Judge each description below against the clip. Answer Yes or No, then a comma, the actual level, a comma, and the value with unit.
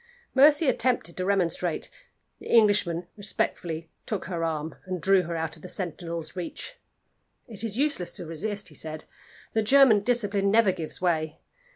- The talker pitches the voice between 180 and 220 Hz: Yes, medium, 185 Hz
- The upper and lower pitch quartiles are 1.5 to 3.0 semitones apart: No, average, 4.5 semitones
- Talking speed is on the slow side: No, average, 160 wpm